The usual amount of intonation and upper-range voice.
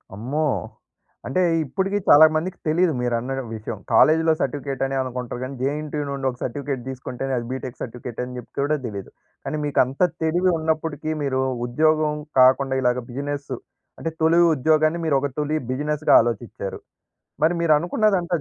No: average, 3.6 semitones; medium, 140 Hz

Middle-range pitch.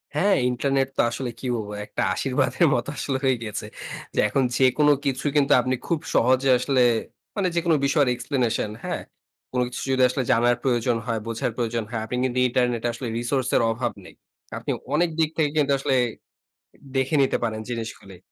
No: low, 130 Hz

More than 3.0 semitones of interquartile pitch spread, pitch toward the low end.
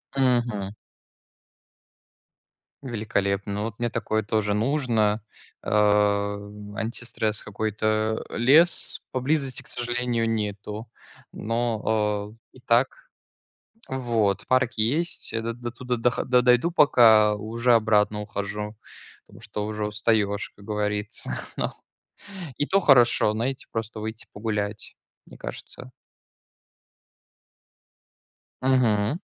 No: average, 2.7 semitones; low, 110 Hz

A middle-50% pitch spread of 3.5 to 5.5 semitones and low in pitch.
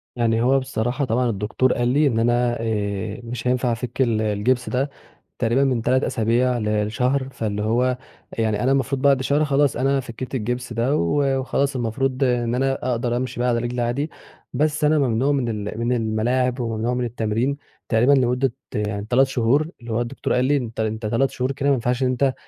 No: average, 2.7 semitones; low, 125 Hz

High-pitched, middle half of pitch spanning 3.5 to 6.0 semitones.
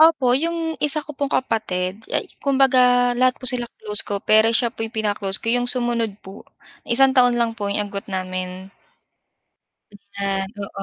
Yes: high, 235 Hz; average, 4.2 semitones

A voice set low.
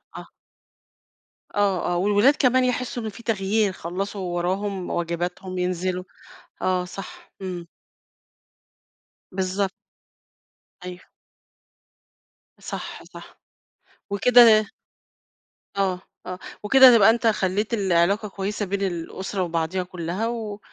No: high, 195 Hz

